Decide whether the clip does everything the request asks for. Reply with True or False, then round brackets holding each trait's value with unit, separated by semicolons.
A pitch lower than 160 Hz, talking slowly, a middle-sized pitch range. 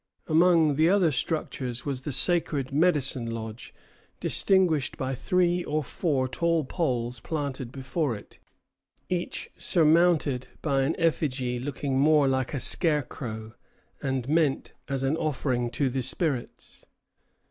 True (140 Hz; 125 wpm; 4.0 semitones)